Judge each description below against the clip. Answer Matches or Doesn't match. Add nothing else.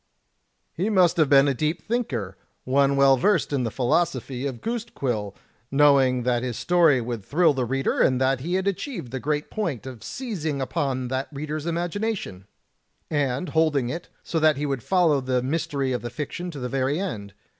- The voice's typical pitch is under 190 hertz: Matches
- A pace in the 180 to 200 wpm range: Matches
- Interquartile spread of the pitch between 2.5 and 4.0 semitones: Doesn't match